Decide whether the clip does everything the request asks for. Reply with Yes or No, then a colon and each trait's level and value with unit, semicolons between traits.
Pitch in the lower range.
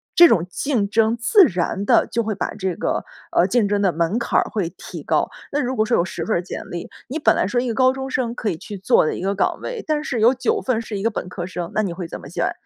No: high, 215 Hz